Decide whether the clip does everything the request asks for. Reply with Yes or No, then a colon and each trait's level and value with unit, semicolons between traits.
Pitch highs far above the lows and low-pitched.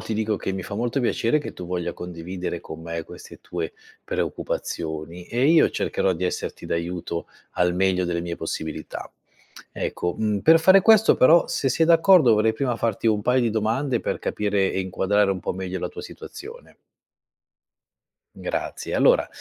Yes: wide, 5.9 semitones; low, 100 Hz